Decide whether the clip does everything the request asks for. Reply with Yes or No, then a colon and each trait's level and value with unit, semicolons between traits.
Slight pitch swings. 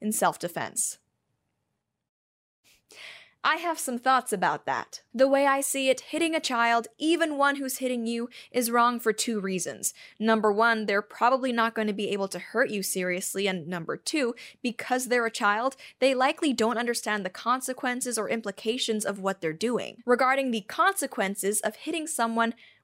No: average, 3.7 semitones